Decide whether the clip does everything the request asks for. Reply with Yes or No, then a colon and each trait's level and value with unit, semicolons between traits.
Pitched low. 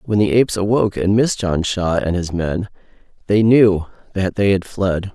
Yes: low, 100 Hz